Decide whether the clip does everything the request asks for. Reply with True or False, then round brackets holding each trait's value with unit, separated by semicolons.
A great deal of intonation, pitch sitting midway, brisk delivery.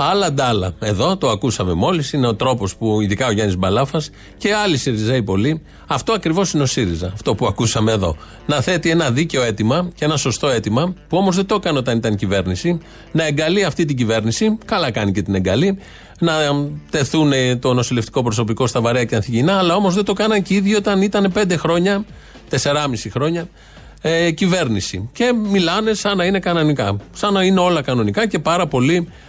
True (7.9 semitones; 145 Hz; 190 wpm)